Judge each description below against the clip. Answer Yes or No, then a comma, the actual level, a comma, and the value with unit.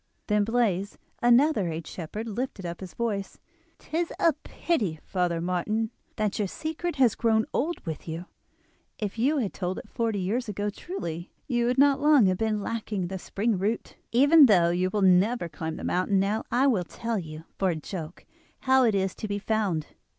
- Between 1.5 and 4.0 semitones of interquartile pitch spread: No, average, 4.8 semitones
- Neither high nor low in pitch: No, high, 210 Hz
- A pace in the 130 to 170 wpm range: No, average, 185 wpm